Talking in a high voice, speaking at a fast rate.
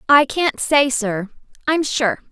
No: very high, 265 Hz; average, 155 wpm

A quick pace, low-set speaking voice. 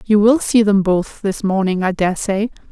No: fast, 220 wpm; high, 200 Hz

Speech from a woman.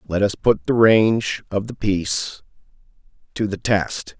No: male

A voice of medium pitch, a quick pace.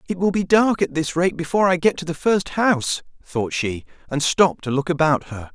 Yes: medium, 165 Hz; fast, 240 wpm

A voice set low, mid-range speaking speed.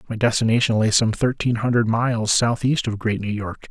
Yes: low, 115 Hz; average, 195 wpm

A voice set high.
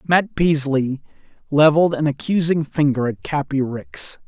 No: medium, 145 Hz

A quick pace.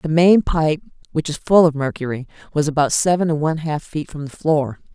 Yes: fast, 220 wpm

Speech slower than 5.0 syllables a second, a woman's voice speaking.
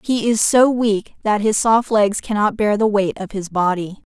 Yes: 4.4 syllables/s; female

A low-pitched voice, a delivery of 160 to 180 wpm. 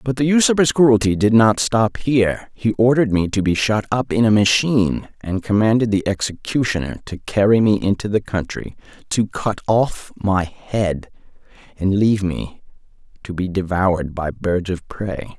Yes: low, 105 Hz; average, 170 wpm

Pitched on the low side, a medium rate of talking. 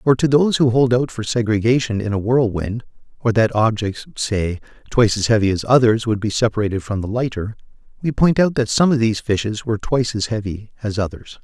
No: low, 115 Hz; fast, 210 wpm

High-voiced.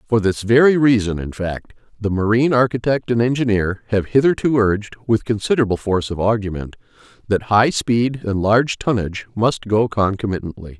No: low, 110 Hz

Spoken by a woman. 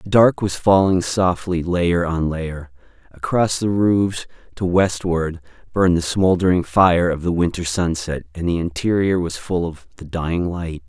No: male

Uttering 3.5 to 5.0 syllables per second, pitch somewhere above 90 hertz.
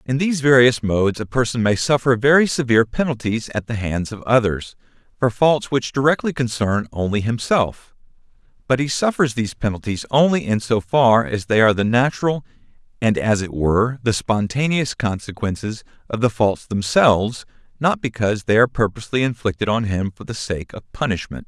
No: 5.5 syllables/s; low, 115 Hz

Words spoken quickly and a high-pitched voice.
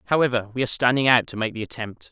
No: fast, 255 wpm; low, 120 Hz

